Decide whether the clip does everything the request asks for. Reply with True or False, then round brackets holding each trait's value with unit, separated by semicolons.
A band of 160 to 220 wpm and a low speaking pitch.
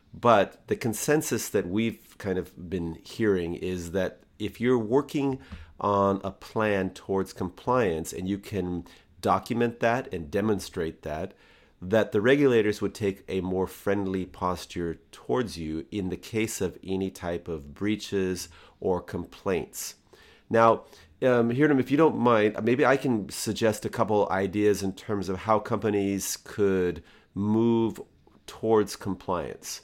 False (145 wpm; 100 Hz)